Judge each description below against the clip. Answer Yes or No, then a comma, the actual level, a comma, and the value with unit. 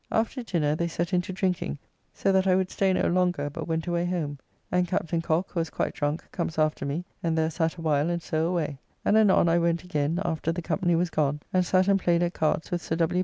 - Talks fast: Yes, fast, 245 wpm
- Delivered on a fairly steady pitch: Yes, narrow, 2.3 semitones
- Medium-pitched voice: Yes, medium, 170 Hz